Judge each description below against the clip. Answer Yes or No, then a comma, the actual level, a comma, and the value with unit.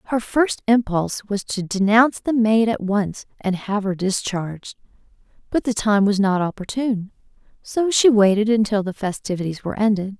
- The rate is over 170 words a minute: No, average, 165 wpm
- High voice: Yes, high, 210 Hz